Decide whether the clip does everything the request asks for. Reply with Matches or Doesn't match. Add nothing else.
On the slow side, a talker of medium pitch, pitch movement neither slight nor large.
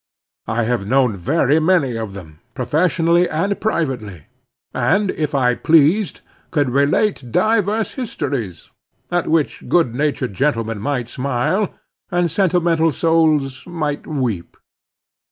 Doesn't match